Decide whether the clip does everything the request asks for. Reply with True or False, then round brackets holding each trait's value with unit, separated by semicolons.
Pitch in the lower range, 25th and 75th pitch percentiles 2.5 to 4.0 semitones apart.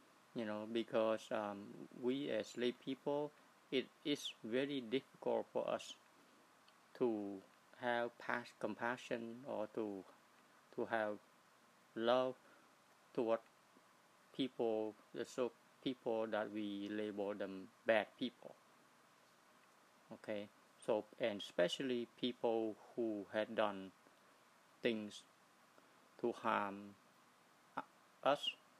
True (115 Hz; 2.8 semitones)